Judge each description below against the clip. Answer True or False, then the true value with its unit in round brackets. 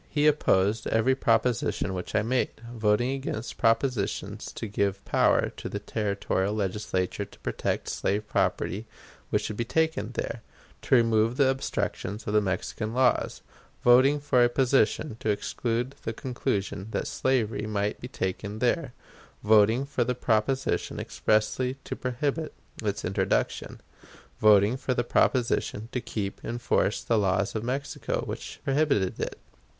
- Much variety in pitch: False (3.6 semitones)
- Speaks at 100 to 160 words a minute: True (145 wpm)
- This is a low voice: True (115 Hz)